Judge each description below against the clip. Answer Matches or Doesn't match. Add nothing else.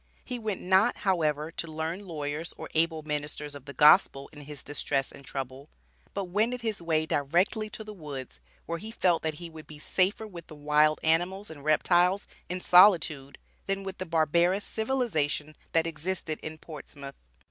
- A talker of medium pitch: Matches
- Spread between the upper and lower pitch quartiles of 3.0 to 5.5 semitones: Matches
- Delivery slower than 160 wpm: Doesn't match